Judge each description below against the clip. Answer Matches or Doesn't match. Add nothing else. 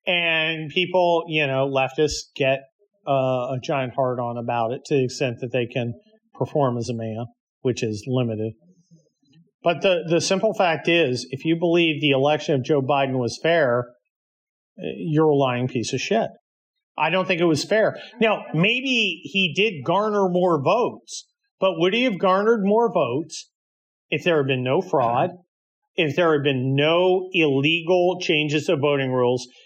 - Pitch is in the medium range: Matches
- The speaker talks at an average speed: Matches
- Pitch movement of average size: Doesn't match